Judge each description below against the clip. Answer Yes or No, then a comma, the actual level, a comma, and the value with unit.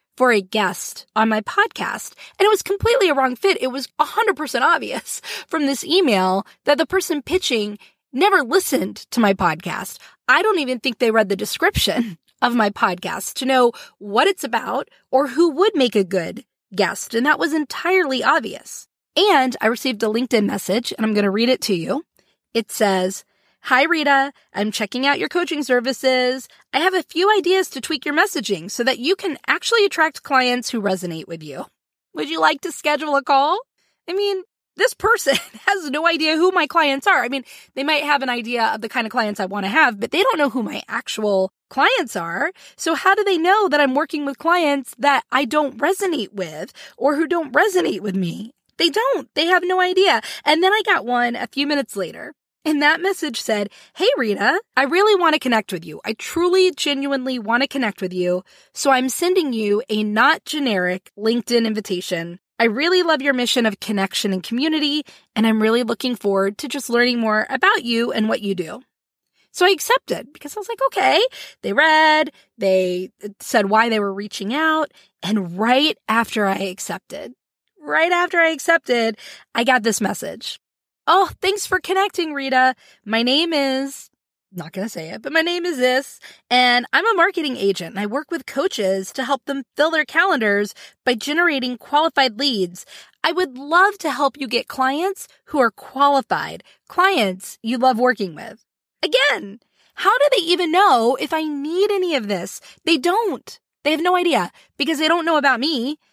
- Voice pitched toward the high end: Yes, very high, 270 Hz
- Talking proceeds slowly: No, average, 195 wpm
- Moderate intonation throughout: No, wide, 7.1 semitones